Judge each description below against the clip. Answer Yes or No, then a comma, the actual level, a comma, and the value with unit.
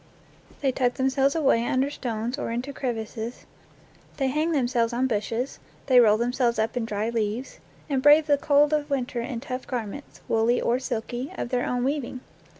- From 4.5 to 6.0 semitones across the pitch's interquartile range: No, average, 2.8 semitones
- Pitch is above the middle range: Yes, very high, 250 Hz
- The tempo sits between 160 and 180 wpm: Yes, average, 175 wpm